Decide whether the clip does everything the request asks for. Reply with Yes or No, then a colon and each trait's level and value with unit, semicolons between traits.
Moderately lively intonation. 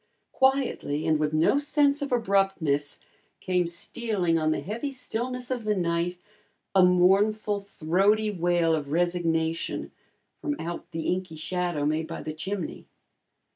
Yes: average, 4.7 semitones